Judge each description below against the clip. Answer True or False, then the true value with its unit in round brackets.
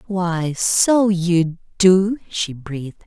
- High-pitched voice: False (180 Hz)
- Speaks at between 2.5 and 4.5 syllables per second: True (2.8 syllables/s)